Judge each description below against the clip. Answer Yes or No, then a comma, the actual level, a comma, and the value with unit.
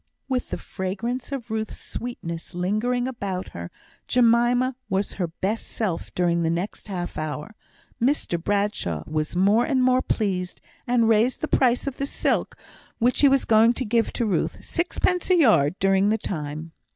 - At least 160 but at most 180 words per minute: Yes, average, 165 wpm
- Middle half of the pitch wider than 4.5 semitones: Yes, wide, 5.4 semitones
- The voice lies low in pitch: No, high, 220 Hz